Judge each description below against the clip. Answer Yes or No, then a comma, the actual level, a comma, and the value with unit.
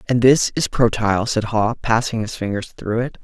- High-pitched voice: No, low, 115 Hz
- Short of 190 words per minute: No, fast, 205 wpm